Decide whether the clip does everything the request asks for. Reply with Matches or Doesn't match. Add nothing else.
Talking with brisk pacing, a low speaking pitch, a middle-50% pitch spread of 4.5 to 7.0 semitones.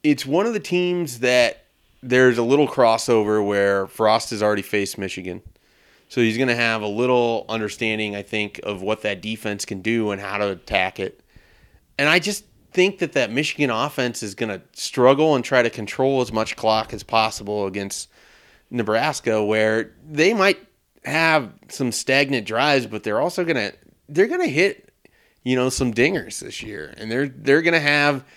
Doesn't match